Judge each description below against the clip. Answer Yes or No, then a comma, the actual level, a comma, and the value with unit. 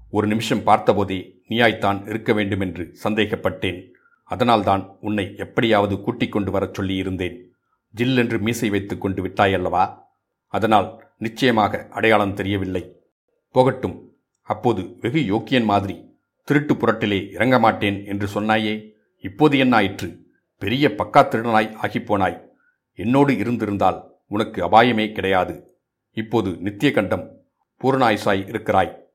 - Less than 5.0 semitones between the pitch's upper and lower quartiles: Yes, narrow, 2.6 semitones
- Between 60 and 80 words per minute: No, average, 100 wpm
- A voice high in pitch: No, low, 105 Hz